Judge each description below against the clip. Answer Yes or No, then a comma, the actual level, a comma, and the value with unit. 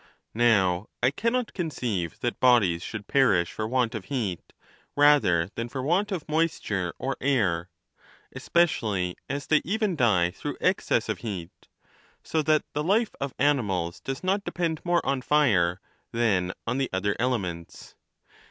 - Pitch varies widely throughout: Yes, wide, 7.9 semitones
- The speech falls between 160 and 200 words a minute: No, average, 150 wpm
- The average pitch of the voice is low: Yes, low, 120 Hz